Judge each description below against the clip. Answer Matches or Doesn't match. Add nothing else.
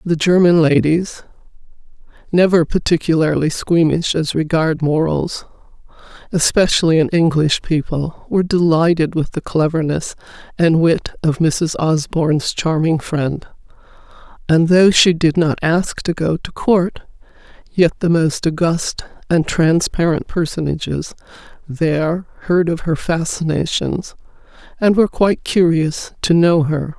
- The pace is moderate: Doesn't match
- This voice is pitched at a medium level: Matches